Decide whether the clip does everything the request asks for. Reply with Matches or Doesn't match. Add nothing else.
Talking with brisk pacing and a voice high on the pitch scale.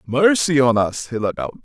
Doesn't match